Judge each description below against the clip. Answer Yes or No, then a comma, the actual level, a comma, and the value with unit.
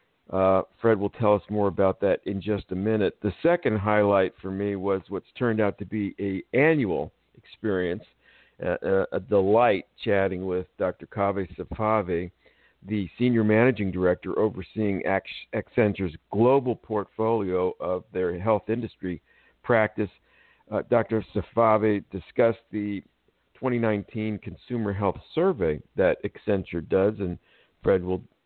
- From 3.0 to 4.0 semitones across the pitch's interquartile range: No, narrow, 2.6 semitones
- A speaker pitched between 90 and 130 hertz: Yes, low, 100 Hz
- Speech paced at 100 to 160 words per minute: Yes, slow, 135 wpm